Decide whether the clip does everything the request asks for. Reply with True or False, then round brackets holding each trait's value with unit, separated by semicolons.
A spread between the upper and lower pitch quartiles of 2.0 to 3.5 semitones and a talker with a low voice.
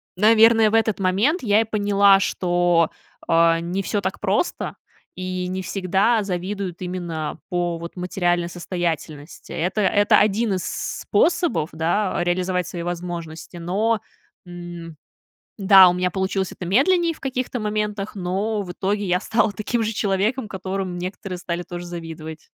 False (3.1 semitones; 185 Hz)